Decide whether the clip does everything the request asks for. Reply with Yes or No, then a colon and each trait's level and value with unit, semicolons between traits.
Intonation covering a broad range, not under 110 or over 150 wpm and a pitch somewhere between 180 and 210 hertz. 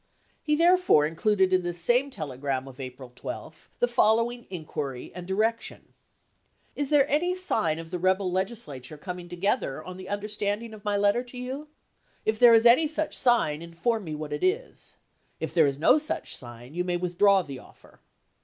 No: wide, 7.3 semitones; average, 195 wpm; high, 190 Hz